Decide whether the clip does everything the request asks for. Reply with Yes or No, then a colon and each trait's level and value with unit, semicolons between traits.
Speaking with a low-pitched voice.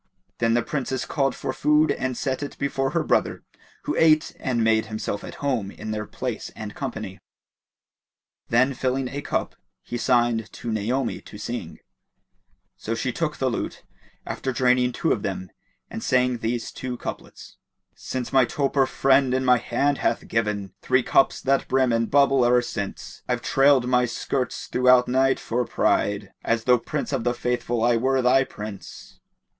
Yes: low, 125 Hz